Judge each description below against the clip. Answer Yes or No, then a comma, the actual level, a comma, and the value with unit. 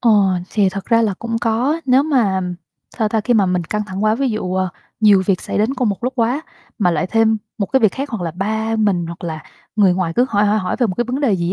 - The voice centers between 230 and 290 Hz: No, high, 215 Hz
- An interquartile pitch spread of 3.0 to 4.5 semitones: Yes, average, 3.8 semitones